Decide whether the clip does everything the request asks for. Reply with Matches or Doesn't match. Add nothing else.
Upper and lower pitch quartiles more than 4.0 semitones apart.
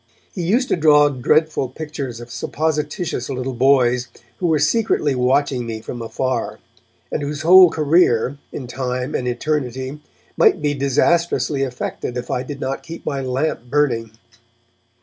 Doesn't match